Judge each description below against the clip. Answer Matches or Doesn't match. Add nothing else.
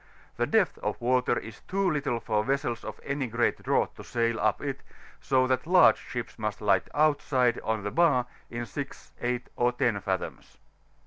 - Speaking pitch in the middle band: Doesn't match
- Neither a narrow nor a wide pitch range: Matches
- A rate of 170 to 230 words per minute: Matches